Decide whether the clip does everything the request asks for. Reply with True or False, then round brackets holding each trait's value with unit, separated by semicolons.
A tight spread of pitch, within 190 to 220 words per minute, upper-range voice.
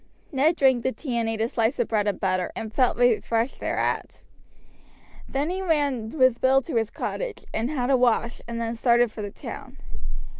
False (3.2 semitones; 195 wpm; 240 Hz)